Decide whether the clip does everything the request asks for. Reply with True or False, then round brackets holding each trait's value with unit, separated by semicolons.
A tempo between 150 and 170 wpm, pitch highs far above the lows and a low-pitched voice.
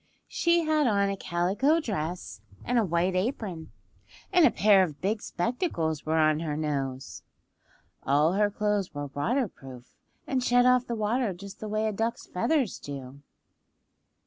False (155 wpm; 7.0 semitones; 195 Hz)